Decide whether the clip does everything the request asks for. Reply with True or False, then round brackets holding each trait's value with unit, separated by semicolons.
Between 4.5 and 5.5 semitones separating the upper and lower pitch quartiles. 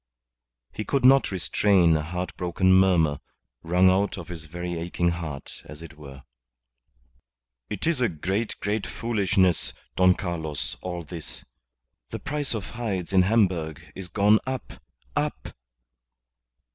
False (3.6 semitones)